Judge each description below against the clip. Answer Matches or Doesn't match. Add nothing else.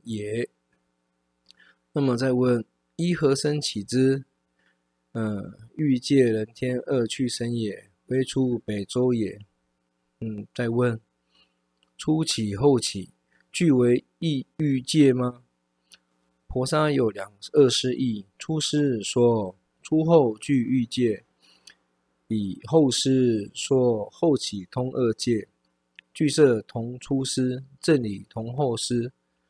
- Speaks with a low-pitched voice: Matches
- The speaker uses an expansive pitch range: Matches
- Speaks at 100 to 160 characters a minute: Matches